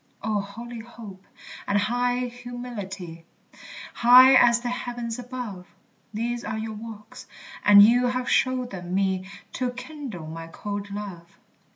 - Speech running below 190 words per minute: Yes, slow, 135 wpm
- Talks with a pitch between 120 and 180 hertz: No, high, 225 Hz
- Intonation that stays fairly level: No, average, 3.6 semitones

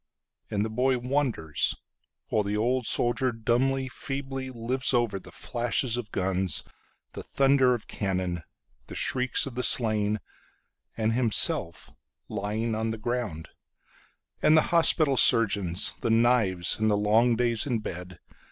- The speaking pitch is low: Yes, low, 115 Hz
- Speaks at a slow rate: Yes, slow, 120 wpm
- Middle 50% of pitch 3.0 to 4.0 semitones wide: Yes, average, 3.5 semitones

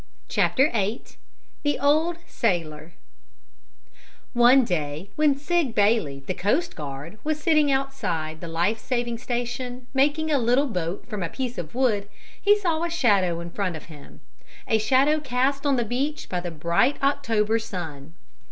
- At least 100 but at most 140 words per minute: No, average, 155 wpm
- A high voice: Yes, high, 235 Hz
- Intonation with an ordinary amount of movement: No, wide, 7.9 semitones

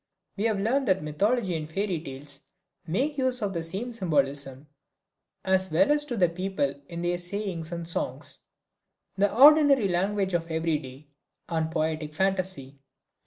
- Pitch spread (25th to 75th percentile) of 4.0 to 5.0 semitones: Yes, average, 4.5 semitones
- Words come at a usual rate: Yes, average, 155 wpm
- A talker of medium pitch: Yes, medium, 180 Hz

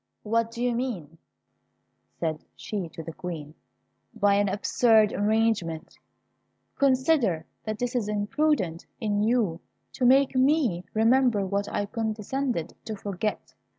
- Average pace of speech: No, slow, 130 wpm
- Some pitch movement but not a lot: Yes, average, 4.5 semitones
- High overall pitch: Yes, high, 215 Hz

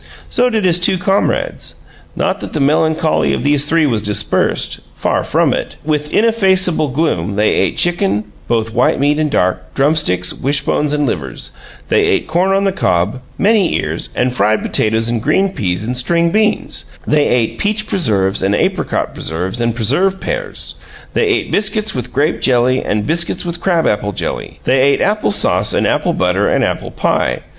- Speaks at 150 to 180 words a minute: Yes, average, 175 wpm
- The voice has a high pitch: No, medium, 145 Hz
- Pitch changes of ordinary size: No, wide, 8.7 semitones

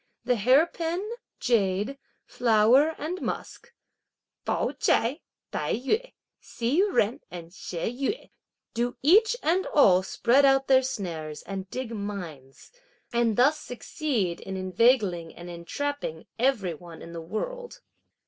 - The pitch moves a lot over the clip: Yes, wide, 7.2 semitones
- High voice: Yes, high, 235 Hz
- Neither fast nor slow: No, slow, 130 wpm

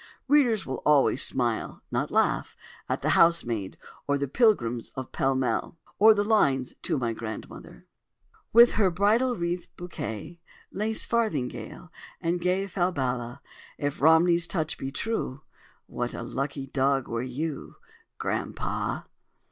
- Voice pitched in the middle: Yes, medium, 150 Hz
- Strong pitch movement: Yes, wide, 6.7 semitones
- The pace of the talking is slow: Yes, slow, 130 wpm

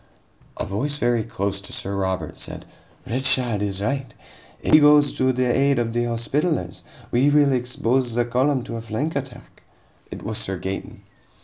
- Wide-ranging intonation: No, average, 3.9 semitones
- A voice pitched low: Yes, low, 120 Hz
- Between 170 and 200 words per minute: Yes, average, 175 wpm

